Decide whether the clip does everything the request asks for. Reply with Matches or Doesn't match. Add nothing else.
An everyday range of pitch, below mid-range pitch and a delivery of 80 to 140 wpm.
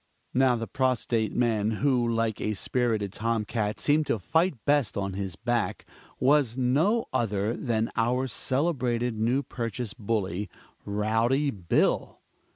Matches